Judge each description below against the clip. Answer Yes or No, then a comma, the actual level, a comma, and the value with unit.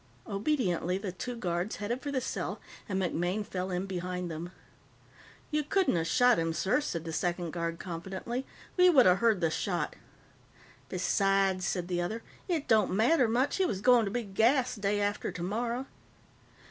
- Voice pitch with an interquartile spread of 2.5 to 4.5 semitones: No, average, 5.3 semitones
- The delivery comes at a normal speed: Yes, average, 170 wpm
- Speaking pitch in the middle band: No, high, 195 Hz